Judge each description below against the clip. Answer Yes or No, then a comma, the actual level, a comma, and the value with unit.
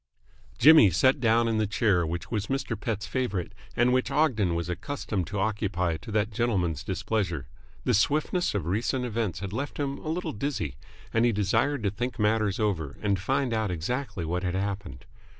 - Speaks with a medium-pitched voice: No, low, 105 Hz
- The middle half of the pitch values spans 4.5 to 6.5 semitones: Yes, average, 5.0 semitones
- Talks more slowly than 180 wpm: No, average, 185 wpm